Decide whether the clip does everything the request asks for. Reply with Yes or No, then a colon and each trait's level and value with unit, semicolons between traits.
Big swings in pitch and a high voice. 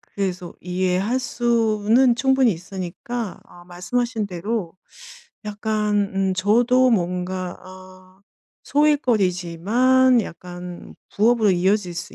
No: average, 4.7 semitones; high, 205 Hz